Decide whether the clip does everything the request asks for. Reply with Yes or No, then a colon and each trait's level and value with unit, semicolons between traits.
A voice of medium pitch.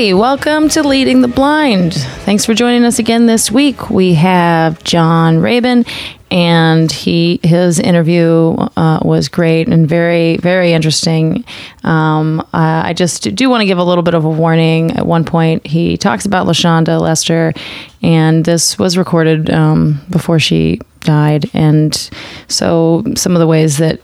Yes: medium, 170 Hz